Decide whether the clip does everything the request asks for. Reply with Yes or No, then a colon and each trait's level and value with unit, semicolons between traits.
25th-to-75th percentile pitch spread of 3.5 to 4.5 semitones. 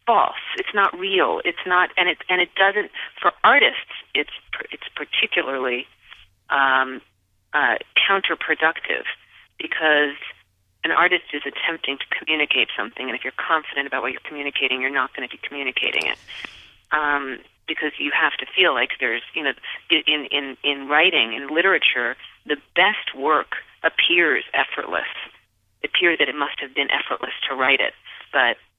No: average, 5.0 semitones